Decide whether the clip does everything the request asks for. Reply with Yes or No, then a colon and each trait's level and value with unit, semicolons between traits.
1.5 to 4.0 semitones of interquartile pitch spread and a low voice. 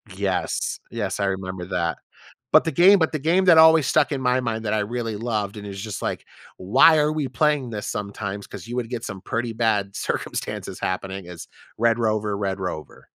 No: average, 4.9 semitones; low, 110 Hz